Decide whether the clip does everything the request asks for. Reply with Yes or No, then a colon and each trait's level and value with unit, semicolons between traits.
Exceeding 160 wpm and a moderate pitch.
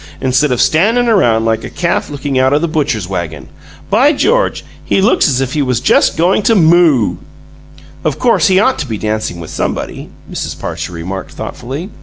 Yes: average, 190 wpm; medium, 145 Hz